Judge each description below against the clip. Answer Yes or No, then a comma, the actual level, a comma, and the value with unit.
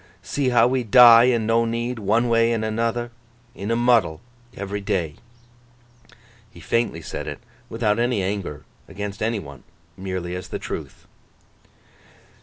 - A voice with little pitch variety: No, average, 3.2 semitones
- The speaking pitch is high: No, low, 115 Hz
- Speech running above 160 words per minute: No, slow, 135 wpm